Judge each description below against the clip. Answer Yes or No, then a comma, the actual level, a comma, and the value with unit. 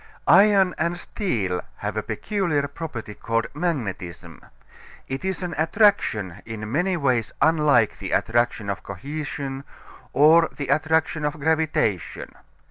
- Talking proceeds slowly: Yes, slow, 125 wpm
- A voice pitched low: No, medium, 145 Hz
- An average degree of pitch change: No, wide, 6.6 semitones